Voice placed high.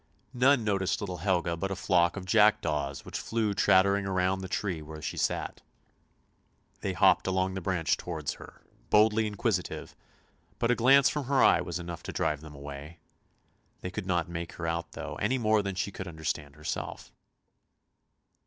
No: very low, 95 Hz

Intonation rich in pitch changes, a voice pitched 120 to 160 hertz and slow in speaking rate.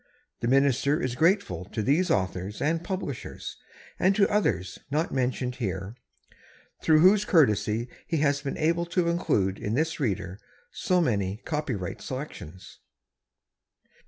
Yes: wide, 8.0 semitones; medium, 140 Hz; slow, 130 wpm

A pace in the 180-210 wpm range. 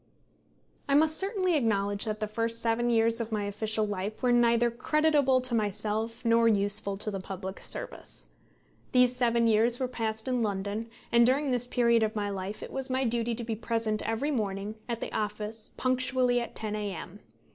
Yes: average, 185 wpm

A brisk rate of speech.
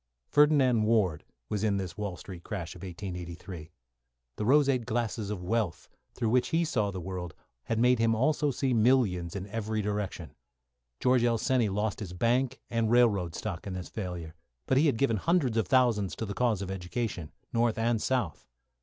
No: average, 180 wpm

